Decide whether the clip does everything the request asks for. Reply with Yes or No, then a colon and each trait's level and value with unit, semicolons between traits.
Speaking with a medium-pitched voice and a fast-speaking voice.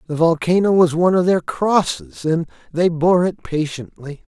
No: medium, 165 Hz; average, 165 wpm